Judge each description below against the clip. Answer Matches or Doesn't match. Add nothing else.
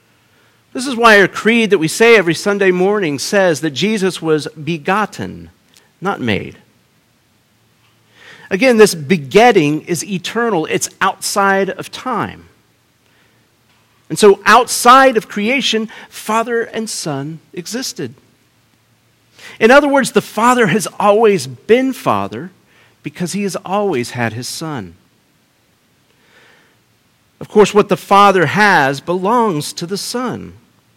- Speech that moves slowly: Matches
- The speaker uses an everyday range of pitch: Doesn't match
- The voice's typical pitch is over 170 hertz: Matches